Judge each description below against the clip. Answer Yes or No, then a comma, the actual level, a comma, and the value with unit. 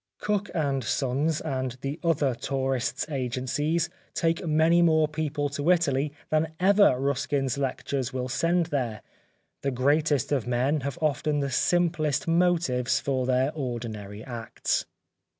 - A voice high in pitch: No, medium, 140 Hz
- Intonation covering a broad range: No, average, 3.7 semitones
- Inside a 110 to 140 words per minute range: Yes, slow, 135 wpm